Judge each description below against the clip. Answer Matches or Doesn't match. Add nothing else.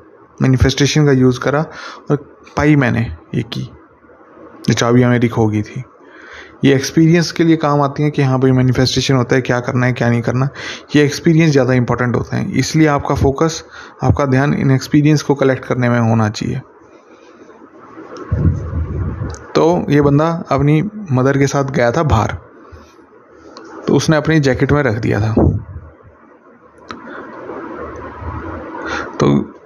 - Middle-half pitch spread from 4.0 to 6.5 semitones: Doesn't match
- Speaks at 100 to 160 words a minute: Matches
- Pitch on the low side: Matches